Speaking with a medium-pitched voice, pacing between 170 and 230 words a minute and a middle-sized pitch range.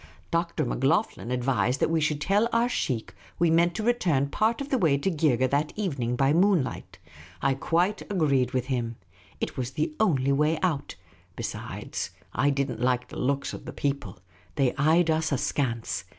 Yes: medium, 145 Hz; average, 180 wpm; average, 4.8 semitones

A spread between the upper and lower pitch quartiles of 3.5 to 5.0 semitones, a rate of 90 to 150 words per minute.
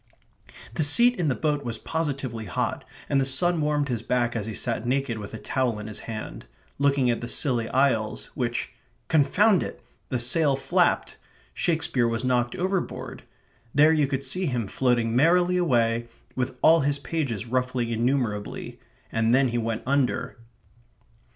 No: average, 3.9 semitones; average, 165 wpm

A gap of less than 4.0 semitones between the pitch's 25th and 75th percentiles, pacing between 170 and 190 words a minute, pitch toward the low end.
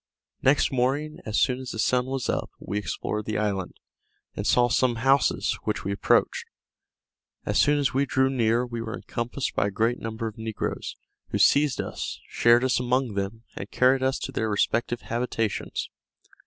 Yes: average, 3.0 semitones; average, 180 wpm; low, 120 Hz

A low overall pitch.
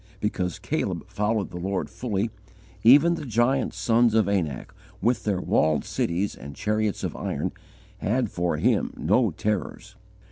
Yes: low, 105 Hz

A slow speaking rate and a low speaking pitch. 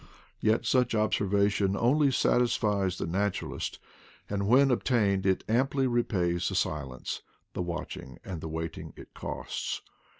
Yes: slow, 130 wpm; low, 100 Hz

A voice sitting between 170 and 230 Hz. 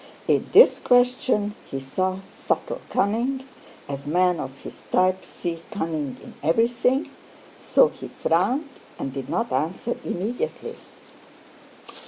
Yes: high, 190 Hz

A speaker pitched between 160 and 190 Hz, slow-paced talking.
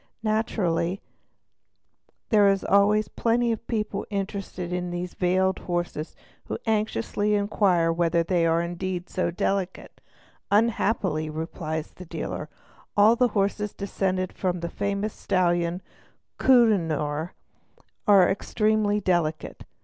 Yes: medium, 185 Hz; slow, 110 wpm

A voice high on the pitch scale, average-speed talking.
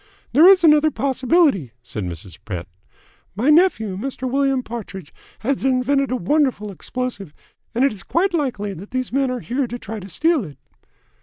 Yes: very high, 255 Hz; average, 170 wpm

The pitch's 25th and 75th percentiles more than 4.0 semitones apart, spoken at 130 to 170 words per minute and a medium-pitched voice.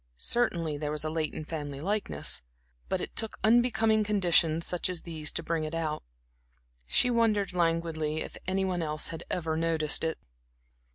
No: average, 3.7 semitones; average, 165 wpm; medium, 165 Hz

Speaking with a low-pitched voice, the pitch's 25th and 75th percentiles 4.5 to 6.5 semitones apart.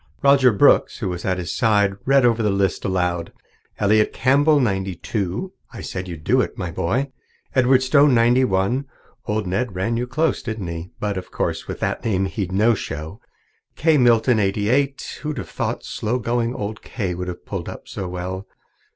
Yes: low, 105 Hz; average, 5.1 semitones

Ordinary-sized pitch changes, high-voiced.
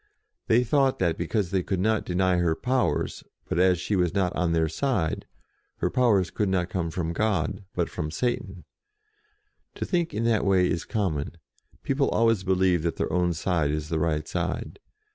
No: average, 4.2 semitones; very low, 90 Hz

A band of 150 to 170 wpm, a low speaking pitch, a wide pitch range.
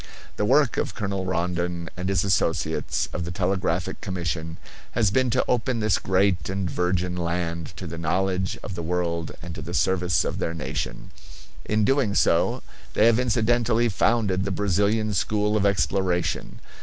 No: average, 165 wpm; very low, 95 Hz; average, 3.4 semitones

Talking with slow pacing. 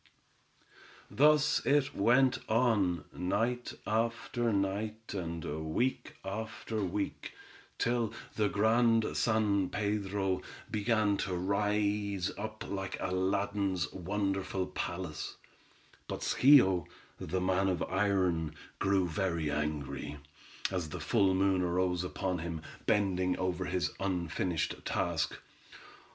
Yes: slow, 105 wpm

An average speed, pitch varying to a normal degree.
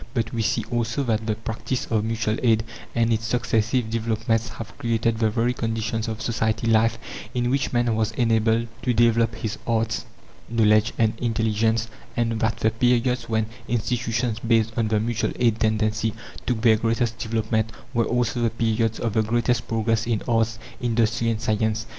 No: average, 170 wpm; narrow, 1.0 semitones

